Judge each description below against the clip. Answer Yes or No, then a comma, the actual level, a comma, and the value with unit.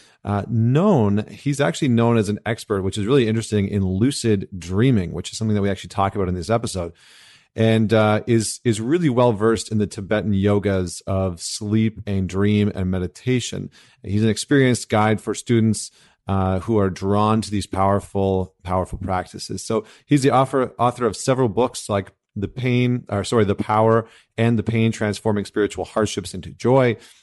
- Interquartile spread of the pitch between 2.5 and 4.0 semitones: Yes, average, 2.9 semitones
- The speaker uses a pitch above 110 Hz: No, low, 105 Hz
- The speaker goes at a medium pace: Yes, average, 180 wpm